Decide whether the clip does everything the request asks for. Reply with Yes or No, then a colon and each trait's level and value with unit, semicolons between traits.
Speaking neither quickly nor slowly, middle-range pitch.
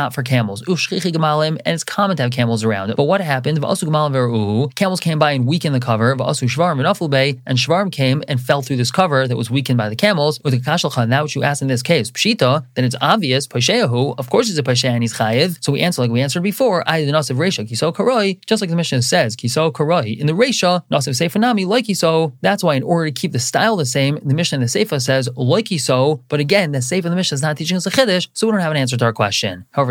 No: fast, 210 wpm; medium, 150 Hz